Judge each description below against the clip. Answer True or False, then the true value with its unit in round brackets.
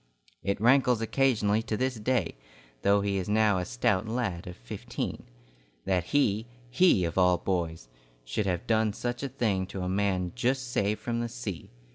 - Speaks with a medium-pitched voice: False (105 Hz)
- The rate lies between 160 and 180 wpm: True (175 wpm)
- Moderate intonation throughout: True (4.5 semitones)